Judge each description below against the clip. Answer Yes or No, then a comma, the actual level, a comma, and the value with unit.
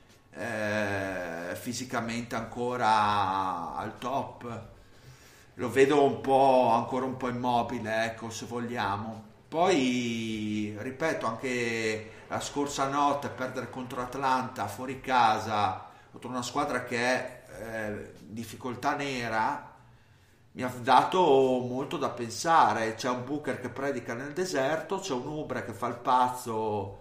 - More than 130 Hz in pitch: No, low, 125 Hz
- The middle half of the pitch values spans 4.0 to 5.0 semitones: No, narrow, 2.5 semitones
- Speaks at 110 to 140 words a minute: Yes, average, 125 wpm